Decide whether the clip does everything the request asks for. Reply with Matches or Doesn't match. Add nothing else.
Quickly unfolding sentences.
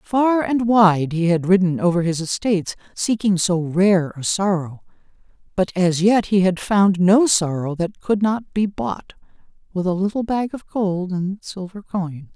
Doesn't match